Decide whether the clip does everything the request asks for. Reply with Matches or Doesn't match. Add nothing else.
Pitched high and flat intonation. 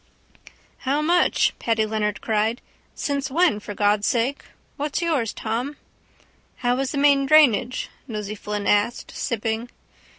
Doesn't match